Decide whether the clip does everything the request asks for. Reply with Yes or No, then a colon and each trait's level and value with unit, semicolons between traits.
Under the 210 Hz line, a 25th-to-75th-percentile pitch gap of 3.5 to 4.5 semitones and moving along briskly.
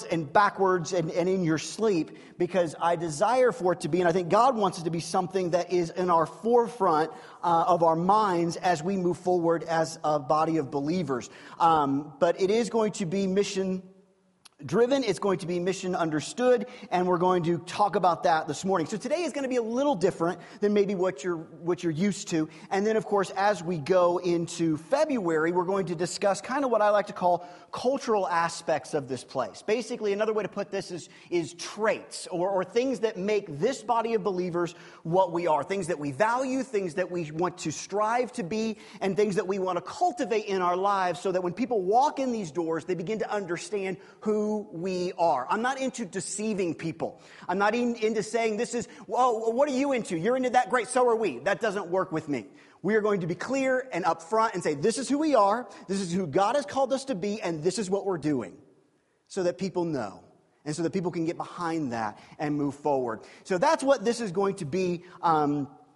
Yes: high, 190 Hz; average, 4.2 semitones; fast, 225 wpm